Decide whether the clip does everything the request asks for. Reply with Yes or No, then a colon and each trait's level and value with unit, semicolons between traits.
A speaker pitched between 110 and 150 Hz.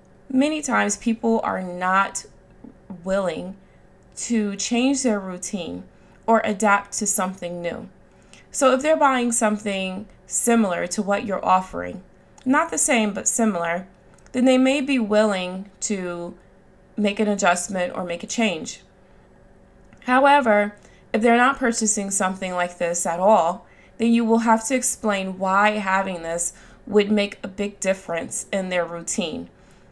No: high, 205 Hz